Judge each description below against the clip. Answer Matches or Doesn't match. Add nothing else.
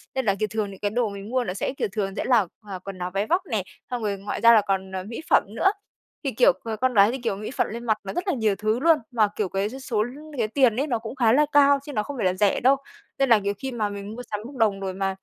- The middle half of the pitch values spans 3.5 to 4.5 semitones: Matches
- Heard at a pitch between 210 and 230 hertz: Matches